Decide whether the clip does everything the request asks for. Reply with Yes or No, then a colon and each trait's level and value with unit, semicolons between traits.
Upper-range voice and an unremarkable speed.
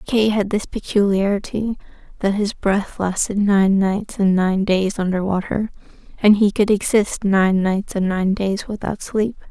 Yes: high, 200 Hz; average, 165 wpm